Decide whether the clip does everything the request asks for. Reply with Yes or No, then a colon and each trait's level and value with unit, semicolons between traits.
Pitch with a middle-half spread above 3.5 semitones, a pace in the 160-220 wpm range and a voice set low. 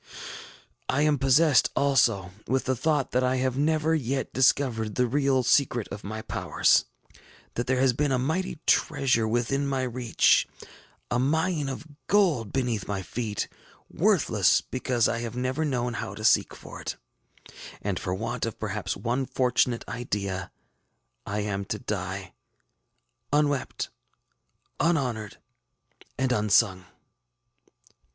No: average, 4.0 semitones; slow, 135 wpm; low, 125 Hz